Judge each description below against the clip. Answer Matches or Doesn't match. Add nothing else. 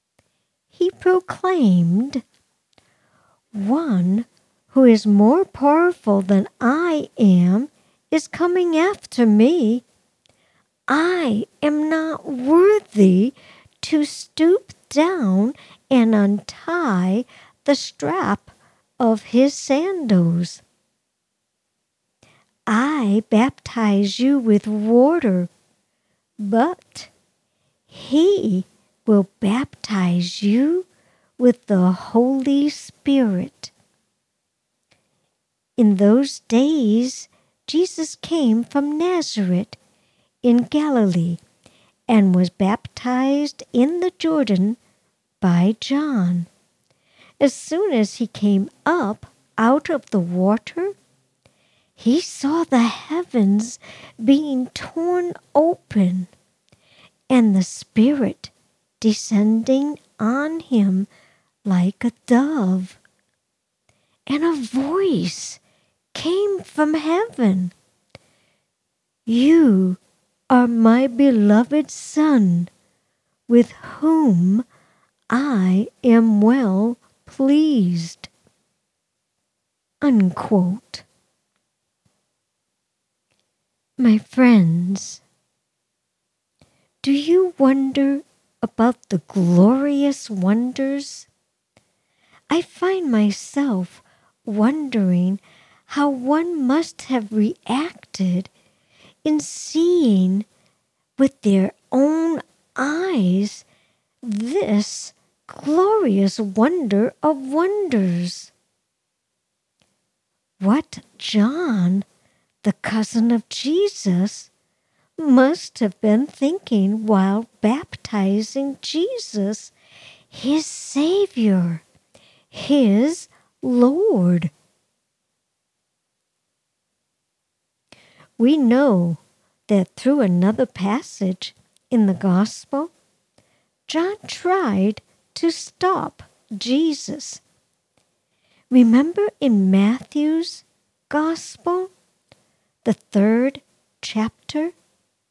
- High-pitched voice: Matches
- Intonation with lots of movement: Matches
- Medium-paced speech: Doesn't match